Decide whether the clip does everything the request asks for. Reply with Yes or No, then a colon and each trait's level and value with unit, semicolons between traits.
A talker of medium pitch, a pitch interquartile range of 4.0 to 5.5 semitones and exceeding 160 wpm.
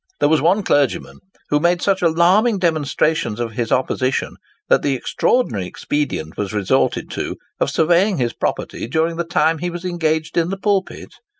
Yes: medium, 160 Hz; average, 4.7 semitones; average, 170 wpm